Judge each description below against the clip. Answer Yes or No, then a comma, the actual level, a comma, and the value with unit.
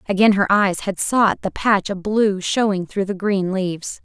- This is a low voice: No, high, 195 Hz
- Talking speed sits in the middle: No, fast, 210 wpm